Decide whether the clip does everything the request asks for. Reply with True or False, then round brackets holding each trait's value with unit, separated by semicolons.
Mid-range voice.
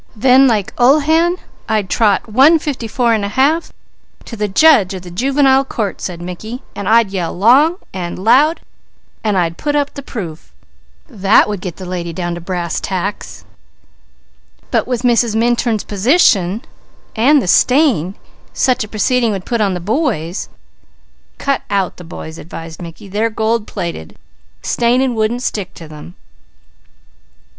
False (215 Hz)